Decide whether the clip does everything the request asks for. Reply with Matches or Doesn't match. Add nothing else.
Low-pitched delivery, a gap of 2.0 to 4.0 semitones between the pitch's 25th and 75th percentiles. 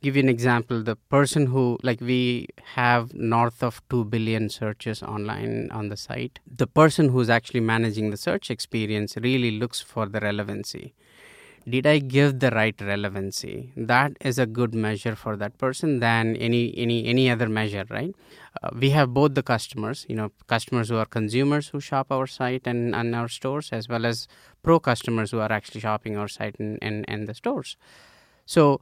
Matches